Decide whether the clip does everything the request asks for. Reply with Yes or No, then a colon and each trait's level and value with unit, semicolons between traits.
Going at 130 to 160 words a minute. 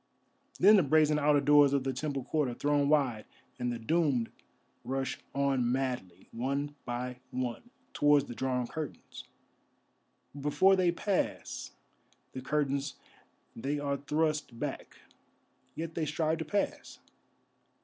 Yes: slow, 135 wpm